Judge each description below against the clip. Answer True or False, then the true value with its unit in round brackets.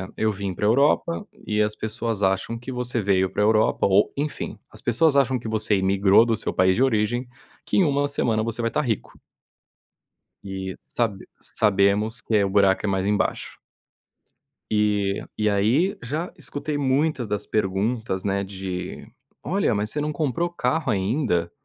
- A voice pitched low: True (110 Hz)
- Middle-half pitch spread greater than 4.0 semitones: True (4.8 semitones)